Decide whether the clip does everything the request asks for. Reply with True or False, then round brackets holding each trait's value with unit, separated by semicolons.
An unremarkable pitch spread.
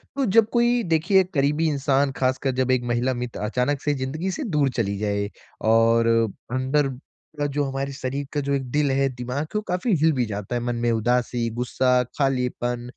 True (3.2 semitones)